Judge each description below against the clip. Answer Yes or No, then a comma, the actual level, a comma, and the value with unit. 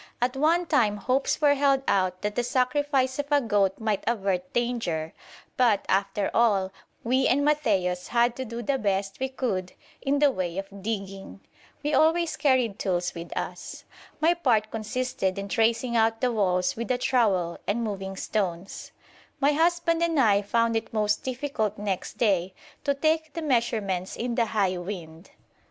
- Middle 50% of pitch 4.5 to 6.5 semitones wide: Yes, average, 5.2 semitones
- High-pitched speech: Yes, high, 225 Hz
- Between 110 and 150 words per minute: No, average, 170 wpm